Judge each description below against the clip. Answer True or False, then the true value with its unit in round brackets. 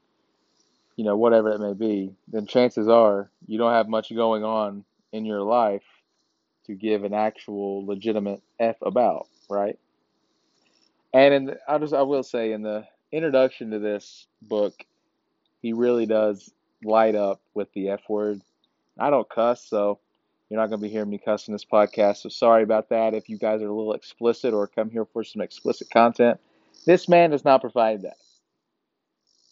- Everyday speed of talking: True (175 wpm)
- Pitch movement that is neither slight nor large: False (2.1 semitones)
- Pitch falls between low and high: False (110 Hz)